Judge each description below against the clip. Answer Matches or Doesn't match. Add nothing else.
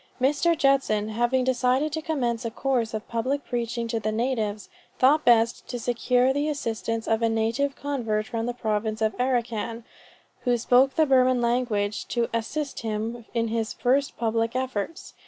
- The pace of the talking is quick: Doesn't match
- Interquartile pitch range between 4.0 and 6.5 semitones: Doesn't match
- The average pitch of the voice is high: Matches